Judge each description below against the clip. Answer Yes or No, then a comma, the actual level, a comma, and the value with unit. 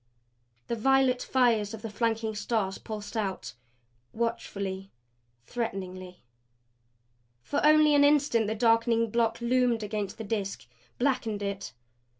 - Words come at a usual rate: No, slow, 120 wpm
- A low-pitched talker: No, high, 225 Hz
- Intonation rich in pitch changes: No, average, 3.0 semitones